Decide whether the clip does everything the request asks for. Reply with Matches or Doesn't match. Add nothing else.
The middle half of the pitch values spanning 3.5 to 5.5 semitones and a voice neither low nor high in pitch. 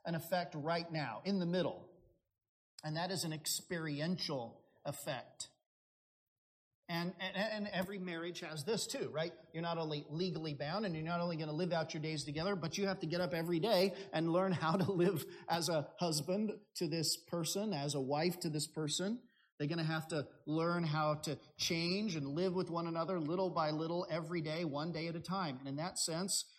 Doesn't match